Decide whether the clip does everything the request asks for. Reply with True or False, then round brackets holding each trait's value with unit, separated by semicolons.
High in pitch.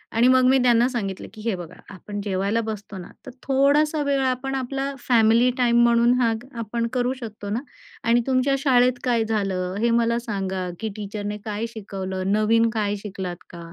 True (230 Hz)